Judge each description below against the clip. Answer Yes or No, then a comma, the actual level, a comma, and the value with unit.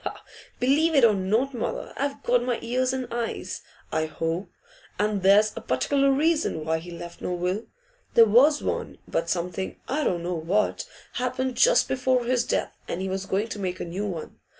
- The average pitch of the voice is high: Yes, high, 215 Hz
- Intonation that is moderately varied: No, wide, 6.1 semitones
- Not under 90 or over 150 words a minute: No, average, 190 wpm